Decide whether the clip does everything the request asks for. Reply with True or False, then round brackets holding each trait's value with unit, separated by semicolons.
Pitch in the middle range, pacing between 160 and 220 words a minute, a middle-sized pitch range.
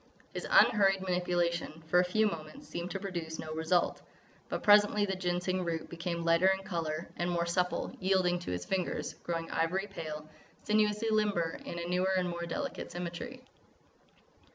False (180 Hz; 165 wpm; 2.2 semitones)